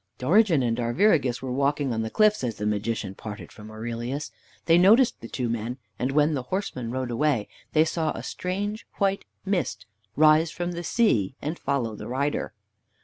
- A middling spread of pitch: No, wide, 6.7 semitones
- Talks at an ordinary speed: Yes, average, 180 wpm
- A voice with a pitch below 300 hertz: Yes, medium, 140 Hz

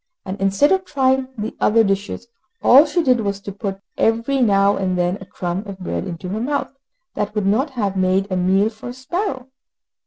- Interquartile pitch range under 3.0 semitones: No, average, 5.0 semitones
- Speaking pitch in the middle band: No, high, 210 Hz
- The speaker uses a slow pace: No, fast, 205 wpm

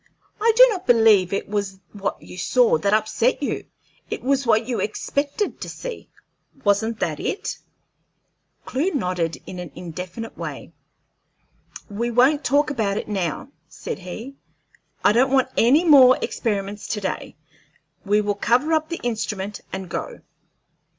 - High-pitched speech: Yes, high, 225 Hz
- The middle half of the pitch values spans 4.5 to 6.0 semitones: Yes, wide, 5.5 semitones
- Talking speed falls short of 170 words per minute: Yes, average, 150 wpm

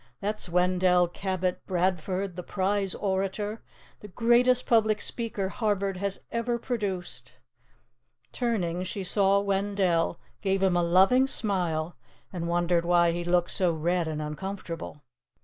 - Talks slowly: Yes, slow, 130 wpm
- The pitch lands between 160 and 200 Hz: Yes, high, 190 Hz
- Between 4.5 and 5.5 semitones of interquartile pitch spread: No, average, 2.7 semitones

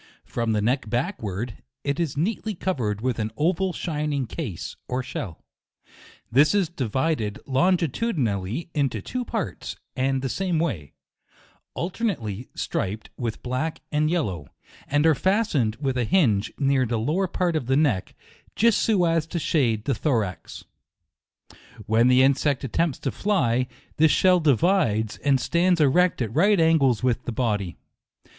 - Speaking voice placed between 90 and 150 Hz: Yes, medium, 140 Hz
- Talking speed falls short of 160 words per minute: Yes, average, 150 wpm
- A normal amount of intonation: No, wide, 6.5 semitones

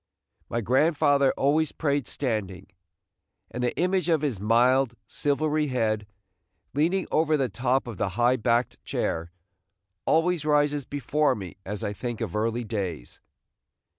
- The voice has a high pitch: No, low, 130 Hz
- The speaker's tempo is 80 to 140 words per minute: Yes, slow, 135 wpm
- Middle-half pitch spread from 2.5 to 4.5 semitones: No, average, 5.0 semitones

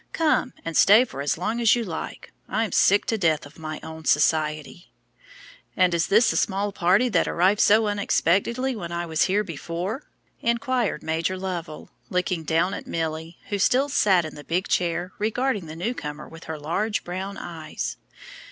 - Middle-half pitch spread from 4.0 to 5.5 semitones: Yes, average, 4.6 semitones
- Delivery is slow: No, average, 180 wpm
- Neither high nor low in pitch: Yes, medium, 180 Hz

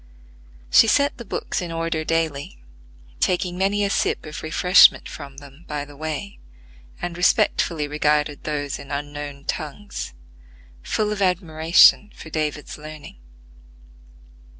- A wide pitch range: No, average, 3.6 semitones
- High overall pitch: No, medium, 155 Hz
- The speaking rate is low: Yes, slow, 125 wpm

